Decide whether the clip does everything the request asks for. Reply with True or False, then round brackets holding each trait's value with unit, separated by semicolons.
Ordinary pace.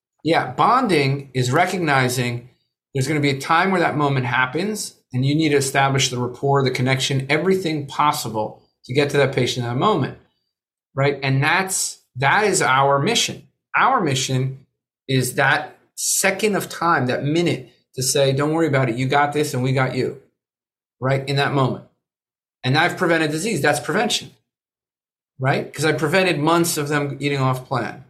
True (175 wpm)